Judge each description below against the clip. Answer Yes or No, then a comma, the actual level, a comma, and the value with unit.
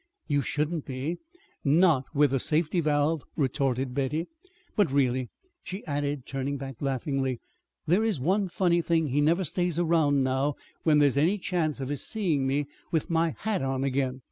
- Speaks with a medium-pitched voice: Yes, medium, 145 Hz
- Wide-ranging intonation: No, average, 3.7 semitones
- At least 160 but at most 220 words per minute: Yes, average, 170 wpm